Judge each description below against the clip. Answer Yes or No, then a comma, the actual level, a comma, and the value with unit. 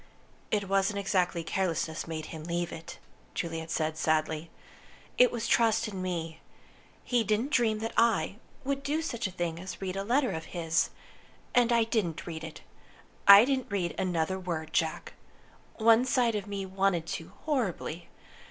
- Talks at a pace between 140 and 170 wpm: Yes, average, 160 wpm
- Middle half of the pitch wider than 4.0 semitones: Yes, wide, 5.5 semitones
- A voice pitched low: No, high, 190 Hz